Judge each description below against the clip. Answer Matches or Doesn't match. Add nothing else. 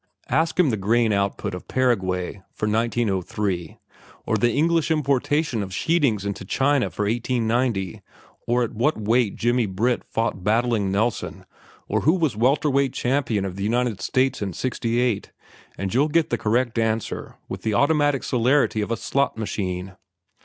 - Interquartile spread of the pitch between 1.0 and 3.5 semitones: Doesn't match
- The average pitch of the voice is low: Matches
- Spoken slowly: Doesn't match